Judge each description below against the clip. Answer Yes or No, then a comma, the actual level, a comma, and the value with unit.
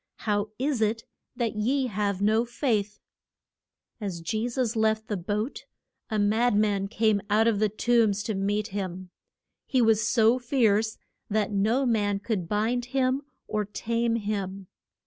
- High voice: Yes, high, 215 Hz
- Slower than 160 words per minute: Yes, average, 150 wpm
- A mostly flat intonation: Yes, narrow, 2.3 semitones